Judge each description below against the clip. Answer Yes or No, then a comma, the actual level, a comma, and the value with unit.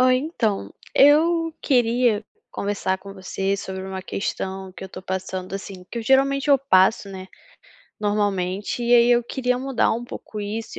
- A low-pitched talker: No, high, 210 Hz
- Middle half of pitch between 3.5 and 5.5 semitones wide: Yes, average, 4.7 semitones